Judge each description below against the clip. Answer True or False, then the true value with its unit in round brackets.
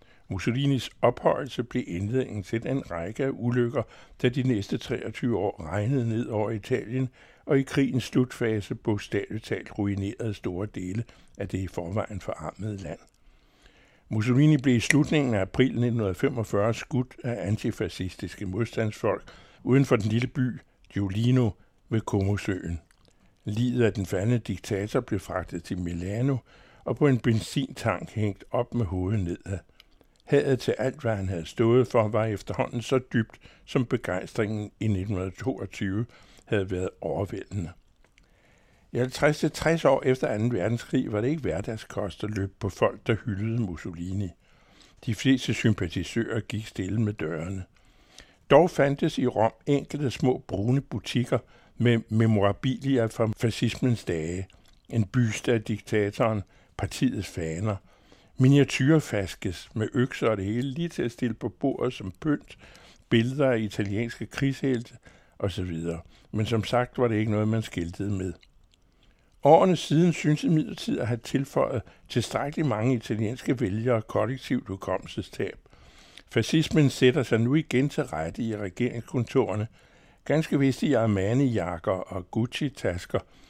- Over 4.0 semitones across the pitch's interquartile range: True (4.4 semitones)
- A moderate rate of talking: False (135 wpm)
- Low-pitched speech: True (115 Hz)